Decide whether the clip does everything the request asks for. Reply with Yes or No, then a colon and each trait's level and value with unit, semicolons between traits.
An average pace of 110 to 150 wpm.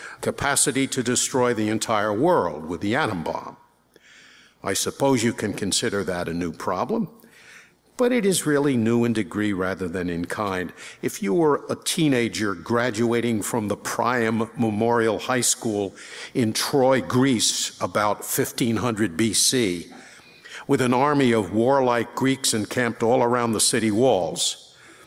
Yes: average, 145 wpm